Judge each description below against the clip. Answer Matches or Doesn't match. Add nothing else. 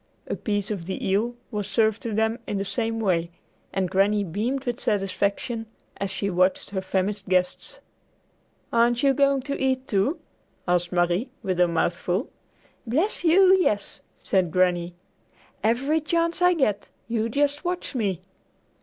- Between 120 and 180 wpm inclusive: Matches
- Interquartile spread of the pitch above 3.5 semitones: Matches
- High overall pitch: Matches